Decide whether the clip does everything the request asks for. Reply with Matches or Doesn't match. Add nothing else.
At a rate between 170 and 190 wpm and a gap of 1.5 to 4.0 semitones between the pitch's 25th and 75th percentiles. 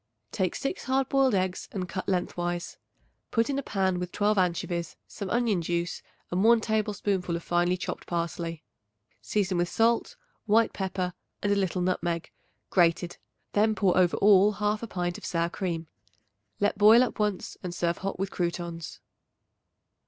Doesn't match